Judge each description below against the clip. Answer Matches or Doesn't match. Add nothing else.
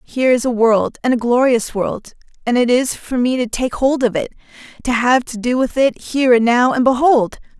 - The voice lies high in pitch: Matches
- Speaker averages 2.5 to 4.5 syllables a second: Doesn't match